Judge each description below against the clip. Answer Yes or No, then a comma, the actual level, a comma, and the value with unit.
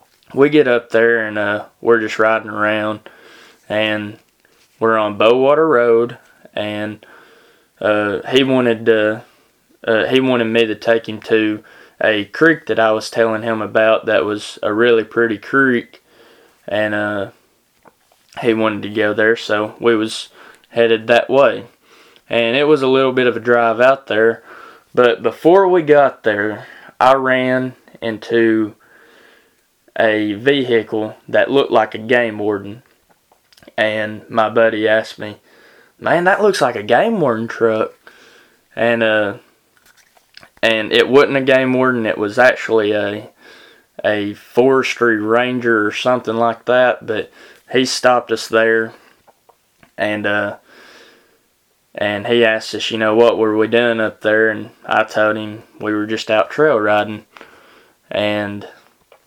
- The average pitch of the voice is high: No, low, 110 Hz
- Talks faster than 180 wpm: No, average, 145 wpm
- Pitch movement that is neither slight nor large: No, narrow, 2.0 semitones